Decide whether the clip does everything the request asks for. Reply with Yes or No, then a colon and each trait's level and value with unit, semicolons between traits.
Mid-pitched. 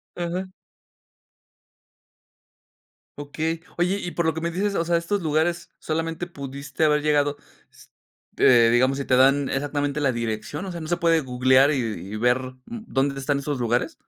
Yes: medium, 145 Hz